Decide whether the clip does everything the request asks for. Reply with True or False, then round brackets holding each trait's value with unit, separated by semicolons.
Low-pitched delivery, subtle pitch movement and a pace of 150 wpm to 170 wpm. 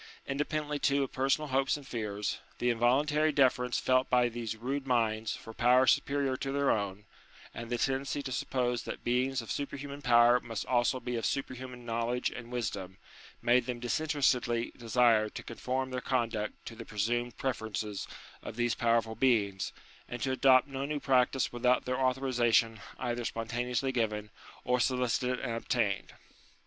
True (125 Hz; 2.3 semitones; 160 wpm)